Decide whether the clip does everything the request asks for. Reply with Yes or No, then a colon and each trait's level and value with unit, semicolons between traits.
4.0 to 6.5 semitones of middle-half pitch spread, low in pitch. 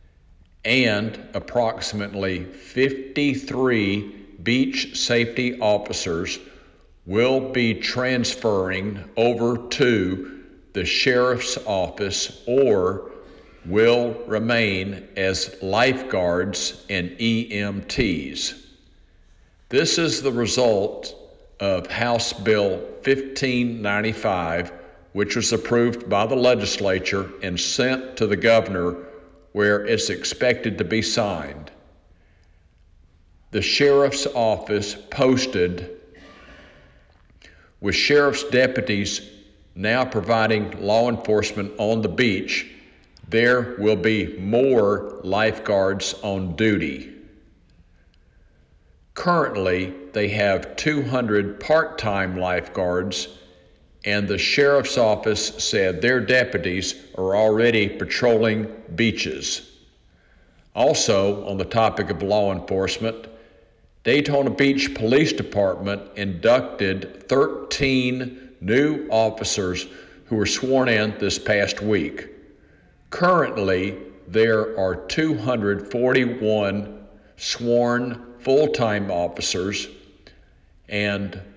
Yes: average, 4.3 semitones; low, 105 Hz